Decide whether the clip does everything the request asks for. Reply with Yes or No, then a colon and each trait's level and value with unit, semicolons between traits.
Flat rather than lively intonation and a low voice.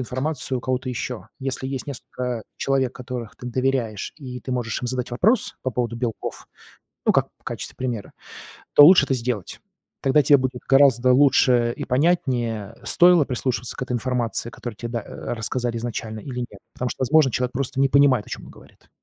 Yes: narrow, 2.1 semitones; low, 125 Hz